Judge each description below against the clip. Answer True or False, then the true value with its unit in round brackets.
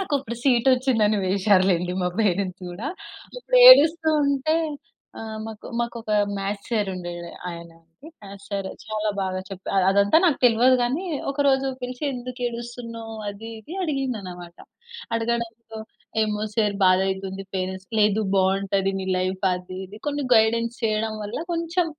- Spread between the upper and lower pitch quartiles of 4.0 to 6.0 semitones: True (4.3 semitones)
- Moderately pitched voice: False (220 Hz)